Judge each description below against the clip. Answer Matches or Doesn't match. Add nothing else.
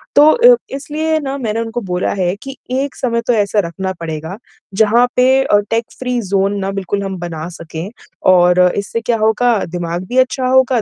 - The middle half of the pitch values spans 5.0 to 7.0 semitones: Matches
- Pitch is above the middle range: Matches